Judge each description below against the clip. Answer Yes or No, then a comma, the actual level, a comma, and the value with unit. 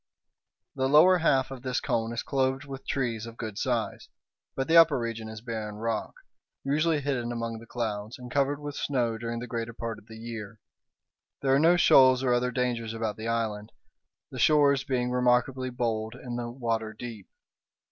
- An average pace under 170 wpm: No, average, 185 wpm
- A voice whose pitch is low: Yes, low, 120 Hz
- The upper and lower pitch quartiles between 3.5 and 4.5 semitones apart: No, average, 2.8 semitones